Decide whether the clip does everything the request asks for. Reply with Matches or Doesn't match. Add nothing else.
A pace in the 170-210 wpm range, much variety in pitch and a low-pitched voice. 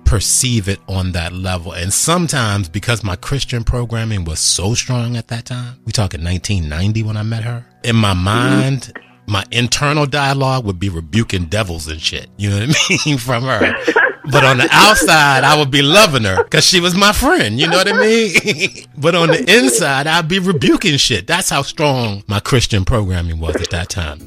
Matches